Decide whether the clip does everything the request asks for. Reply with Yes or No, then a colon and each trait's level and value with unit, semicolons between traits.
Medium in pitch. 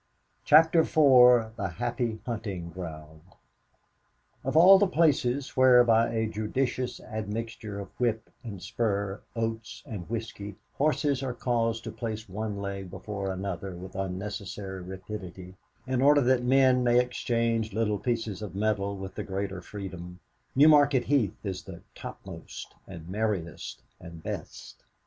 No: low, 110 Hz